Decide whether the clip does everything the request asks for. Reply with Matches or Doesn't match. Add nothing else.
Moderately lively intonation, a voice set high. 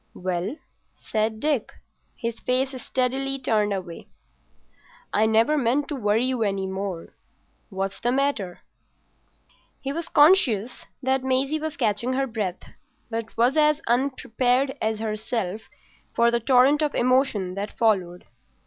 Matches